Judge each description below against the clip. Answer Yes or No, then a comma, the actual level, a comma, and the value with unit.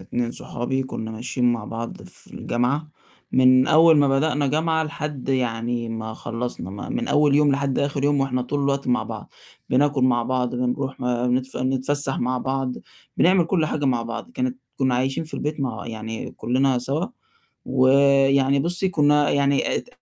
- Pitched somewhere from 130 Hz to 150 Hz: Yes, low, 135 Hz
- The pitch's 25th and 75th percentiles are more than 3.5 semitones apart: No, average, 2.9 semitones